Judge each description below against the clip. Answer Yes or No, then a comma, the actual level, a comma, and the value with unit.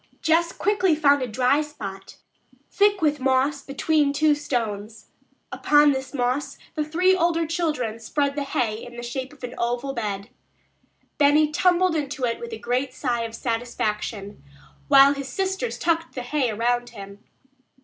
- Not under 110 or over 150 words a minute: No, average, 160 wpm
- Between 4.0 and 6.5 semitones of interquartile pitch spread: Yes, average, 4.3 semitones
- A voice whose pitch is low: No, very high, 275 Hz